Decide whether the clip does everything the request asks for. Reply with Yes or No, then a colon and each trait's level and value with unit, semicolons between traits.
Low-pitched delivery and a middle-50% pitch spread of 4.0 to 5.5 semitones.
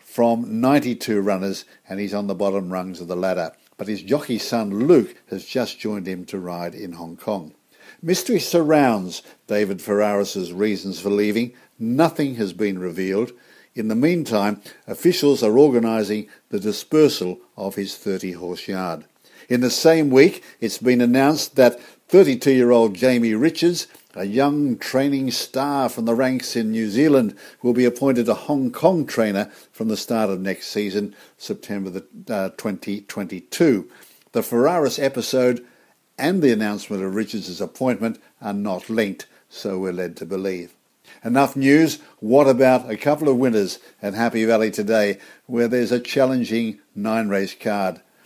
Yes: low, 110 Hz; average, 4.7 semitones